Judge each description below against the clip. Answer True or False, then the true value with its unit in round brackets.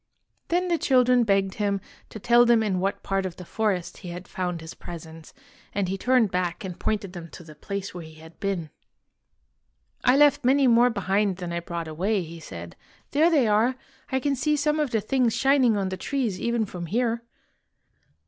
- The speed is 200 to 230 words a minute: True (205 wpm)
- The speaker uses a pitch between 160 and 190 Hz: False (200 Hz)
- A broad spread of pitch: True (5.9 semitones)